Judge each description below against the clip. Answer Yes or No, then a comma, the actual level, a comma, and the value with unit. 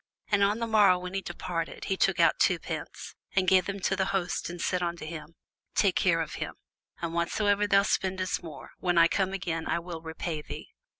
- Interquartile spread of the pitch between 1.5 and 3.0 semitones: Yes, narrow, 2.6 semitones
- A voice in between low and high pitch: Yes, medium, 180 Hz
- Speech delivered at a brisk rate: Yes, fast, 215 wpm